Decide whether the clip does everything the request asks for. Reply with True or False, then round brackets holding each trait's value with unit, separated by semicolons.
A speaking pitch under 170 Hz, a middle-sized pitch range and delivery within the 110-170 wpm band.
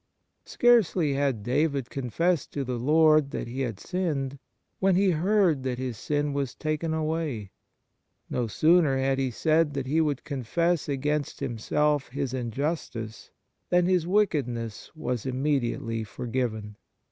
True (140 Hz; 4.3 semitones; 140 wpm)